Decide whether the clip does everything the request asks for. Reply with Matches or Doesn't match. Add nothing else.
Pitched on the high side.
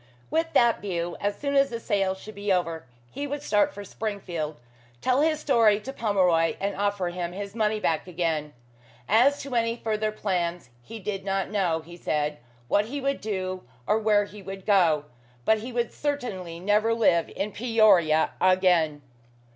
Matches